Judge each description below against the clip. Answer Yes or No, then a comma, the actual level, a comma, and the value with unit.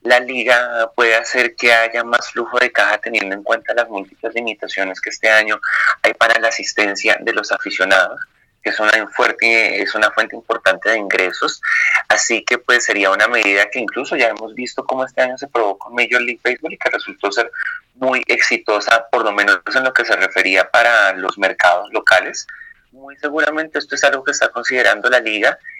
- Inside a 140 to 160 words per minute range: No, average, 195 wpm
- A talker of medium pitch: No, low, 120 Hz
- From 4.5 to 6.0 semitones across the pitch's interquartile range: No, average, 3.7 semitones